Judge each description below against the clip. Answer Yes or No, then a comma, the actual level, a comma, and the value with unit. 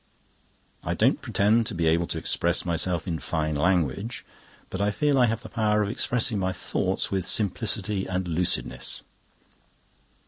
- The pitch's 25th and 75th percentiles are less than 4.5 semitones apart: Yes, average, 4.1 semitones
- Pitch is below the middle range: Yes, very low, 95 Hz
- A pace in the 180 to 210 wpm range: No, average, 160 wpm